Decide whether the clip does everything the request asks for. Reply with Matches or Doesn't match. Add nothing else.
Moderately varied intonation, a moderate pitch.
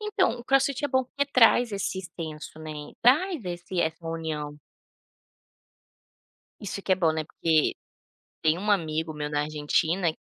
Doesn't match